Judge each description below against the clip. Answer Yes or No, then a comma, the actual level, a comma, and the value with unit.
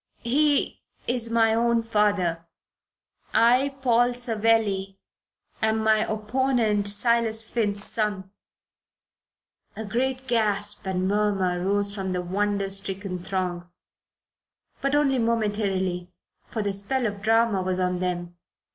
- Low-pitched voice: No, high, 210 Hz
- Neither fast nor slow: No, slow, 115 wpm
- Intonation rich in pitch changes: No, average, 3.2 semitones